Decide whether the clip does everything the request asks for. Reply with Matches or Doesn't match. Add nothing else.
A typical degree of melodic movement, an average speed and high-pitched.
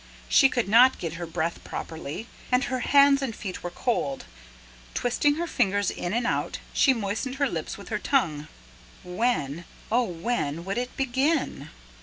Doesn't match